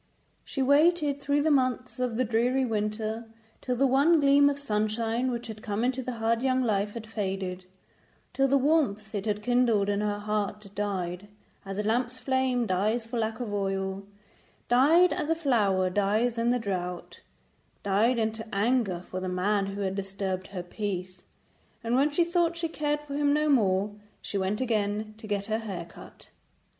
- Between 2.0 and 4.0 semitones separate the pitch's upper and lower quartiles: No, average, 4.4 semitones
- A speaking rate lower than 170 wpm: No, average, 180 wpm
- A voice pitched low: No, high, 225 Hz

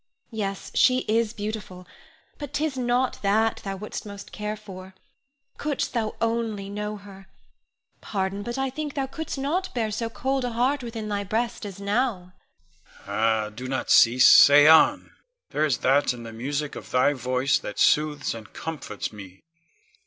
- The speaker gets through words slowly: No, average, 165 wpm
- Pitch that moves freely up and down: Yes, wide, 8.2 semitones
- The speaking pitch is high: Yes, high, 205 Hz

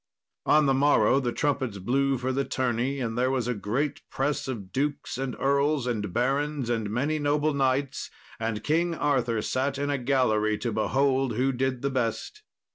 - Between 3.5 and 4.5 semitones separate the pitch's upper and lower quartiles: No, average, 2.8 semitones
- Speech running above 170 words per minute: Yes, average, 180 wpm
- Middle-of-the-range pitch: No, low, 130 Hz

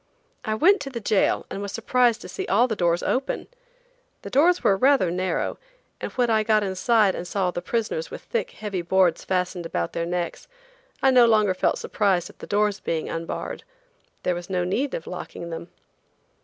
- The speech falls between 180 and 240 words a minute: Yes, average, 195 wpm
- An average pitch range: Yes, average, 4.9 semitones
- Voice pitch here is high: Yes, high, 200 Hz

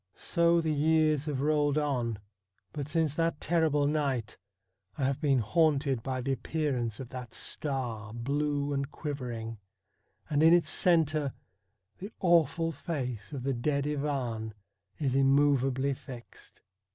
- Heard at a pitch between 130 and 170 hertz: Yes, medium, 140 Hz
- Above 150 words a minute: No, slow, 135 wpm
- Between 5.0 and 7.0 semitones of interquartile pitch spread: No, average, 3.1 semitones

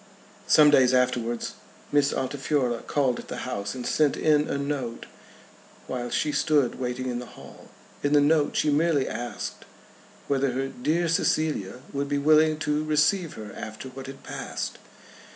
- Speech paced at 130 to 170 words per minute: Yes, average, 160 wpm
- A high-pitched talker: No, medium, 140 Hz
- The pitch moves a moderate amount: Yes, average, 3.1 semitones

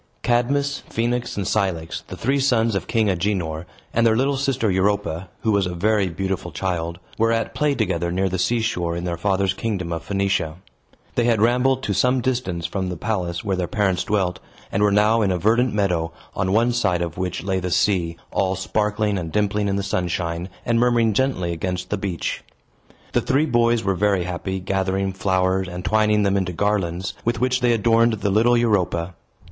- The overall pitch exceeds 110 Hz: No, low, 100 Hz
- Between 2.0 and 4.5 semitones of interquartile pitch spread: Yes, average, 4.0 semitones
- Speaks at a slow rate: No, average, 195 wpm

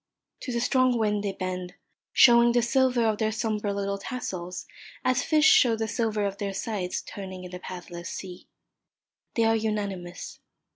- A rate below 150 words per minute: No, average, 165 wpm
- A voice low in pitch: No, high, 210 Hz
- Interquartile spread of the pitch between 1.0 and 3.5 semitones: No, average, 4.0 semitones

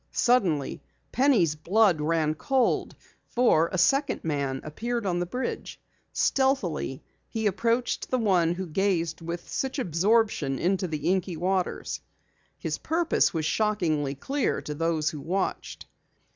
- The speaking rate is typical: No, slow, 130 wpm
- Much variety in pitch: Yes, wide, 6.4 semitones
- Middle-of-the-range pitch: Yes, medium, 180 Hz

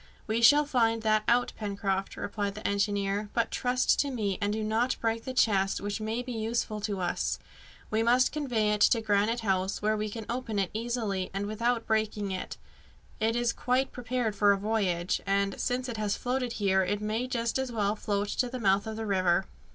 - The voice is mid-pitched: No, high, 215 Hz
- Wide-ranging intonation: No, average, 2.8 semitones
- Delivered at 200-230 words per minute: Yes, fast, 205 wpm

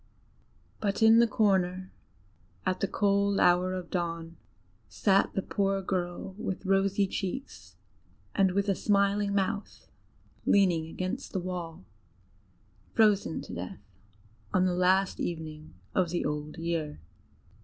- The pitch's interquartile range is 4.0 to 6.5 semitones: No, narrow, 2.4 semitones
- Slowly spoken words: Yes, slow, 125 wpm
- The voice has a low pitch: No, medium, 185 Hz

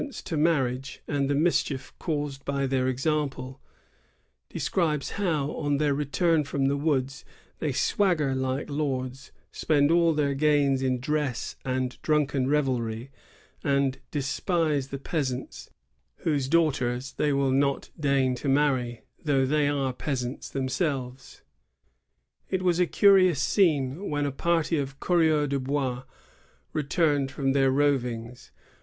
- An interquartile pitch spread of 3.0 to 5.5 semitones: No, narrow, 2.4 semitones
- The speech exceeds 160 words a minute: No, slow, 135 wpm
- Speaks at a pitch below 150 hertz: Yes, medium, 140 Hz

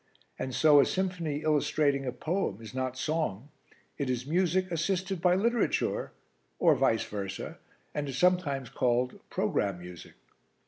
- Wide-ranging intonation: Yes, wide, 5.9 semitones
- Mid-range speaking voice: Yes, medium, 145 Hz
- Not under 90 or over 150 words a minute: Yes, average, 140 wpm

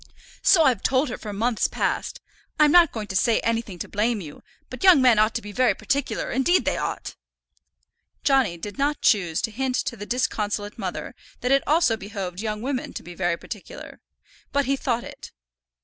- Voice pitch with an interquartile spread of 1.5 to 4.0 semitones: No, average, 4.6 semitones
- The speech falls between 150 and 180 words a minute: No, average, 195 wpm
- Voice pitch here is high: Yes, high, 230 Hz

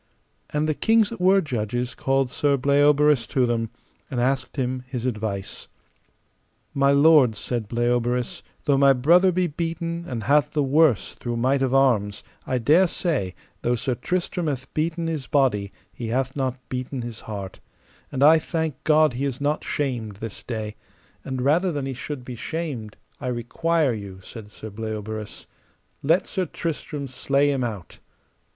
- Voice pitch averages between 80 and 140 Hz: Yes, low, 135 Hz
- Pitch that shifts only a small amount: No, average, 4.1 semitones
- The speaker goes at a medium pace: Yes, average, 160 wpm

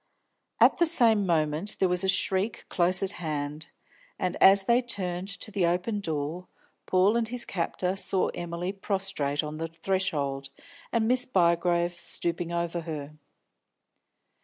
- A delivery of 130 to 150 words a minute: Yes, average, 145 wpm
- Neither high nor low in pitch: Yes, medium, 180 Hz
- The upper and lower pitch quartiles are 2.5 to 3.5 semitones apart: Yes, average, 3.1 semitones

